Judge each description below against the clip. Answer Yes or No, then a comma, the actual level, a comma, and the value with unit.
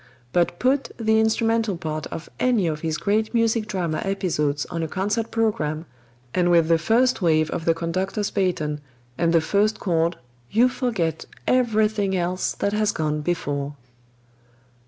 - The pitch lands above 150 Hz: Yes, medium, 185 Hz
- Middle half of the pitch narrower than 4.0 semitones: No, average, 5.1 semitones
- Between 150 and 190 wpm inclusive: Yes, average, 155 wpm